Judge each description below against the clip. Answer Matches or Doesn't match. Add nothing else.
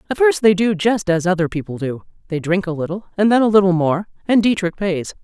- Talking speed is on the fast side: Matches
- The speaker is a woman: Matches